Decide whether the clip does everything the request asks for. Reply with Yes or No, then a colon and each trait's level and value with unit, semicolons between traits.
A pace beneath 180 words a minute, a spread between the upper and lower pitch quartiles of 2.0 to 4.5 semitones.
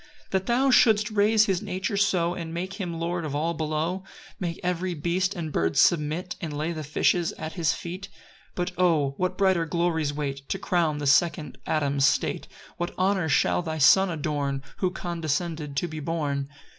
No: average, 185 wpm; average, 3.3 semitones